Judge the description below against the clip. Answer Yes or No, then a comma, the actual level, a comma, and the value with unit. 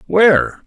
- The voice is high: No, medium, 180 Hz